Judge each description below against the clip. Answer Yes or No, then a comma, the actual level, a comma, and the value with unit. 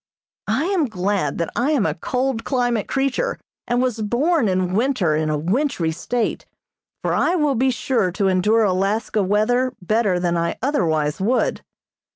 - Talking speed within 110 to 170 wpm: Yes, average, 165 wpm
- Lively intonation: Yes, wide, 5.9 semitones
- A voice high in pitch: Yes, high, 220 Hz